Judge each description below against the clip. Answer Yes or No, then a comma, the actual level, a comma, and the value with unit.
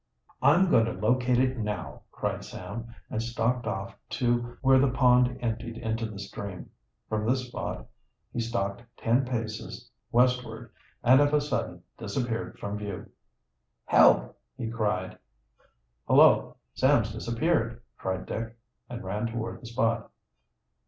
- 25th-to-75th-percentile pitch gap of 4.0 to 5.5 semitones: No, narrow, 2.4 semitones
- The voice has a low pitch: Yes, low, 115 Hz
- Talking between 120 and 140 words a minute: Yes, slow, 135 wpm